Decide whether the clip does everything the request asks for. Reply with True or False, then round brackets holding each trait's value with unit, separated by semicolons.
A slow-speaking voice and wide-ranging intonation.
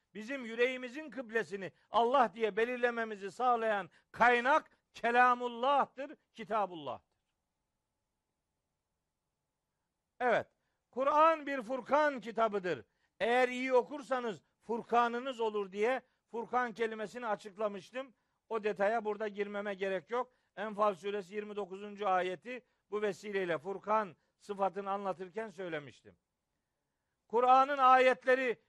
False (90 wpm; 3.7 semitones)